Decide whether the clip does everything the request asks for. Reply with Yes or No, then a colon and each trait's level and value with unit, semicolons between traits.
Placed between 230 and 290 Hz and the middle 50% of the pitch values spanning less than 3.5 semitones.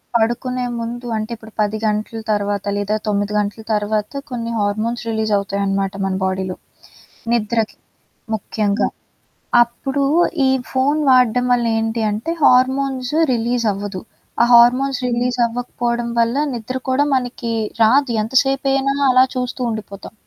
Yes: high, 235 Hz; average, 3.1 semitones